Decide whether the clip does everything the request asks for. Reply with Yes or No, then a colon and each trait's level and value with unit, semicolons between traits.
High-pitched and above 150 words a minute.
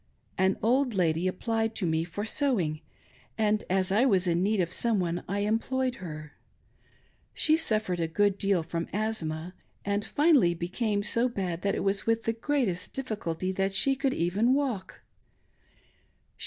Yes: high, 200 Hz; average, 165 wpm